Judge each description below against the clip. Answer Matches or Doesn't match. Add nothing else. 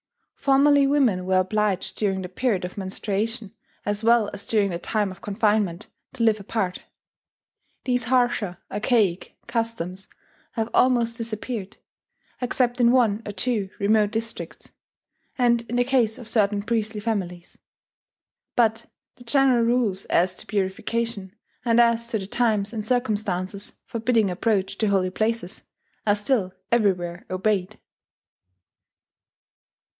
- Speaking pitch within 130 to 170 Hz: Doesn't match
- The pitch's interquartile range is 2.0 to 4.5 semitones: Matches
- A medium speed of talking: Doesn't match